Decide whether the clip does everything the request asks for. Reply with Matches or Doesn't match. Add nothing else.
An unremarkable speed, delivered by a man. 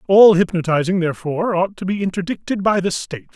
Matches